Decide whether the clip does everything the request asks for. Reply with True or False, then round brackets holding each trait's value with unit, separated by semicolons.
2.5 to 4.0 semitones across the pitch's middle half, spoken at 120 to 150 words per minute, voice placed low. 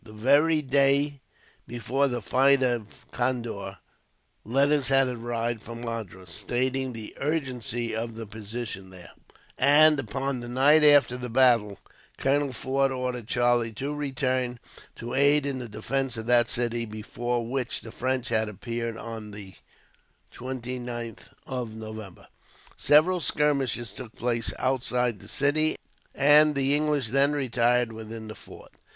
True (3.1 semitones; 140 wpm; 125 Hz)